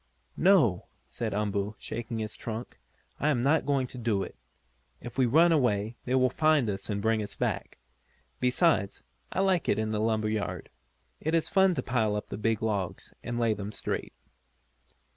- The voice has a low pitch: Yes, low, 115 Hz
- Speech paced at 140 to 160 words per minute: No, average, 180 wpm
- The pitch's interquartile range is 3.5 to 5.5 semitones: Yes, average, 4.2 semitones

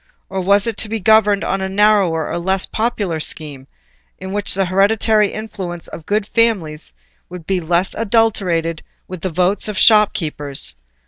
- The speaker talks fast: No, average, 165 wpm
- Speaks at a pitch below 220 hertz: Yes, high, 190 Hz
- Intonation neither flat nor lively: Yes, average, 3.7 semitones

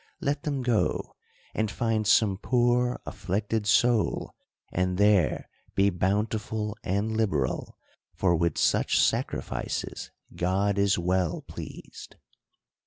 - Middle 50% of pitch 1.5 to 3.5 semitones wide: Yes, average, 3.2 semitones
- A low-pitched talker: Yes, low, 105 Hz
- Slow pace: Yes, slow, 110 wpm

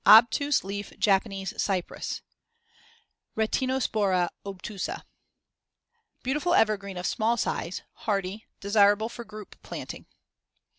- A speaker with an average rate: No, slow, 90 wpm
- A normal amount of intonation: Yes, average, 3.0 semitones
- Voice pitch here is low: No, high, 210 Hz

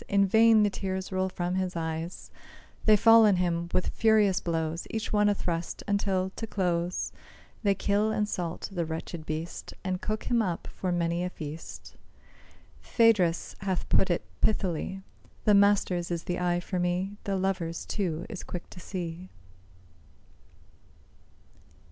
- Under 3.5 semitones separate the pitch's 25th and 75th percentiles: Yes, average, 2.8 semitones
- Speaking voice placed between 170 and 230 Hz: Yes, medium, 185 Hz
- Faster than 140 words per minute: Yes, average, 155 wpm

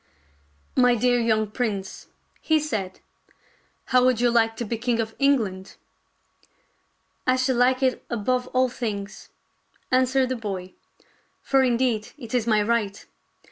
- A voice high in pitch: Yes, high, 235 Hz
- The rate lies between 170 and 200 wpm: No, average, 155 wpm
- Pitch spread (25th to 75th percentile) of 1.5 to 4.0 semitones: Yes, average, 3.0 semitones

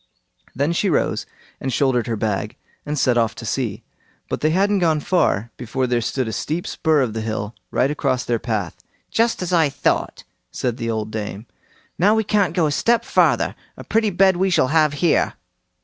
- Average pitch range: No, wide, 7.0 semitones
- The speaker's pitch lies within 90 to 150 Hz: Yes, medium, 140 Hz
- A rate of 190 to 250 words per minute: Yes, average, 195 wpm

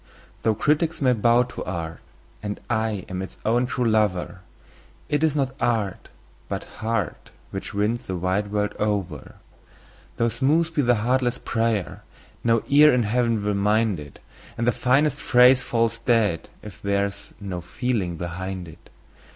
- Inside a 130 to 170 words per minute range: Yes, average, 160 wpm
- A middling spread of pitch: Yes, average, 3.8 semitones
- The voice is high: No, low, 110 Hz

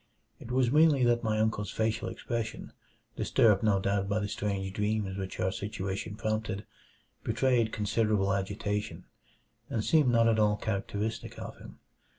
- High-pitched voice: No, low, 110 Hz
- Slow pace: No, average, 150 wpm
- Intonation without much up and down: Yes, narrow, 2.3 semitones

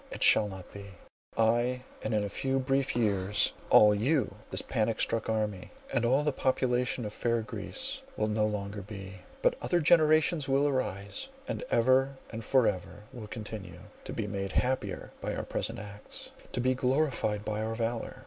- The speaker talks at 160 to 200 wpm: Yes, average, 175 wpm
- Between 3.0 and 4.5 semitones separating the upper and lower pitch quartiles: Yes, average, 4.0 semitones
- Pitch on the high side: No, low, 115 Hz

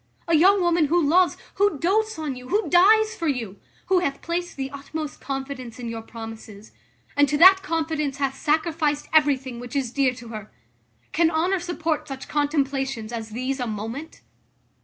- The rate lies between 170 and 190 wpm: Yes, average, 175 wpm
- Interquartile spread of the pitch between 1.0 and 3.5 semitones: No, average, 4.8 semitones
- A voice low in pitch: No, very high, 290 Hz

